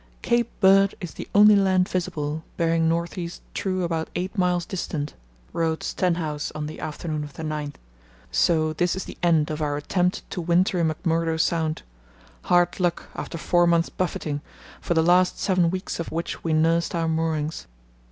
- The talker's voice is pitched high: No, medium, 170 Hz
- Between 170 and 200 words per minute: Yes, average, 175 wpm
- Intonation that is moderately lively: No, narrow, 2.2 semitones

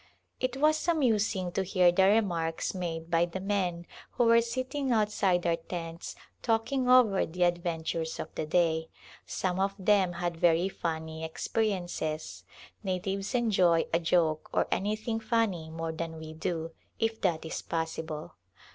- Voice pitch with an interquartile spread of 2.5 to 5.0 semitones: Yes, average, 4.7 semitones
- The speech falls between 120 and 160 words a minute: Yes, average, 145 wpm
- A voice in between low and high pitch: Yes, medium, 180 Hz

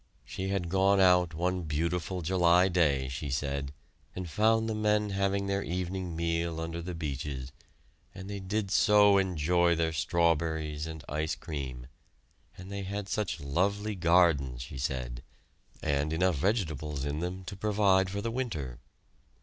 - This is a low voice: Yes, very low, 85 Hz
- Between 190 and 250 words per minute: No, average, 150 wpm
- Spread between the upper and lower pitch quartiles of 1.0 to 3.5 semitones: No, average, 4.3 semitones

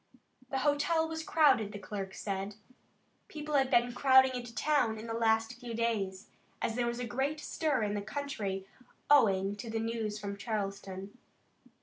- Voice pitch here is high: Yes, high, 230 Hz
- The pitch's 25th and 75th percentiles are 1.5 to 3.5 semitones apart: No, average, 4.7 semitones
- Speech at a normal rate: Yes, average, 165 wpm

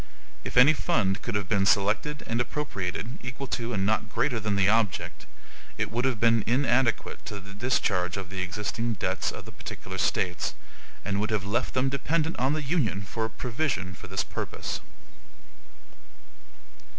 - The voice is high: No, low, 110 Hz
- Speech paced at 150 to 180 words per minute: Yes, average, 170 wpm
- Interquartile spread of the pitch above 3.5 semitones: Yes, average, 4.2 semitones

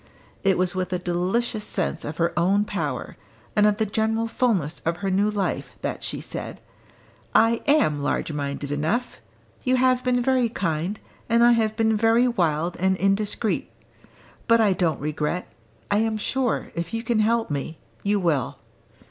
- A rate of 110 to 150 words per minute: No, average, 170 wpm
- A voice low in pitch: No, high, 205 Hz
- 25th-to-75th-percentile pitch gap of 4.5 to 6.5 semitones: Yes, average, 5.1 semitones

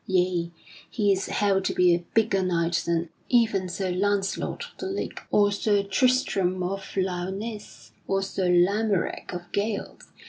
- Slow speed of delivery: No, average, 150 wpm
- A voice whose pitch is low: No, high, 195 Hz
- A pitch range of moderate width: No, narrow, 2.2 semitones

